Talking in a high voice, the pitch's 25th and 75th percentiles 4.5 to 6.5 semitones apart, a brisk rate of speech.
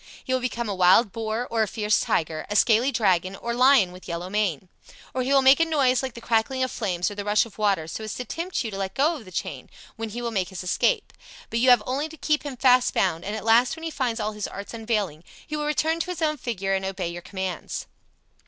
Yes: high, 225 Hz; average, 5.1 semitones; fast, 260 wpm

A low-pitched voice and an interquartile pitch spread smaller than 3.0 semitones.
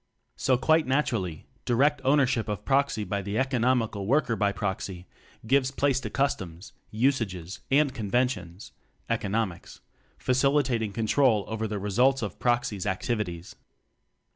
No: low, 115 Hz; average, 4.8 semitones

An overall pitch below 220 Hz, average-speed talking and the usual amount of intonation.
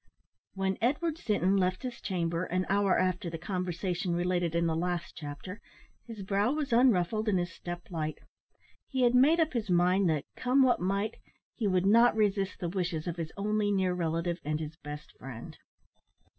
Yes: medium, 185 Hz; average, 180 wpm; average, 3.8 semitones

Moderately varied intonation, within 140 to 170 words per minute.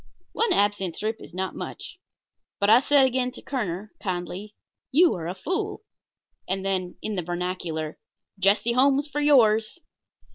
No: wide, 6.1 semitones; average, 150 wpm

